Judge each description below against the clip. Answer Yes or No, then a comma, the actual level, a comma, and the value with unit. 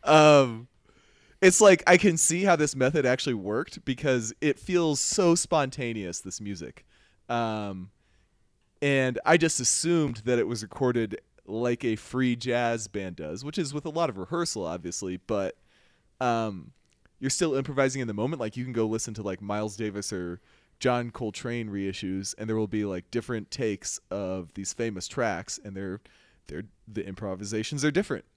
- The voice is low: Yes, low, 115 Hz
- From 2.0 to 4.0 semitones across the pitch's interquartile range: No, wide, 5.5 semitones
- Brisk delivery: No, average, 170 wpm